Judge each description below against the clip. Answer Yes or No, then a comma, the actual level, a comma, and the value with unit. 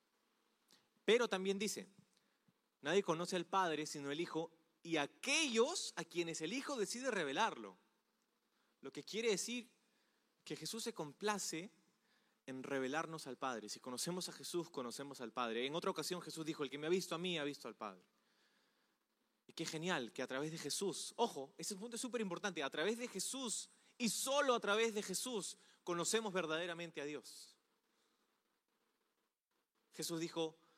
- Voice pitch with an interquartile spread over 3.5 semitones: Yes, average, 5.2 semitones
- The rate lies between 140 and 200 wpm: Yes, average, 160 wpm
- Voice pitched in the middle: Yes, medium, 175 Hz